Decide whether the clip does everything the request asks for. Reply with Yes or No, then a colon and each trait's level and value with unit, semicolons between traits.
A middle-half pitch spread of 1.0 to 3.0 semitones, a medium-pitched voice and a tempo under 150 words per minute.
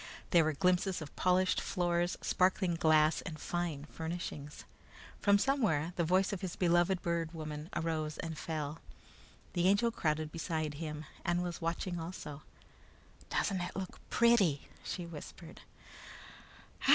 Yes: average, 2.7 semitones; medium, 170 Hz; slow, 135 wpm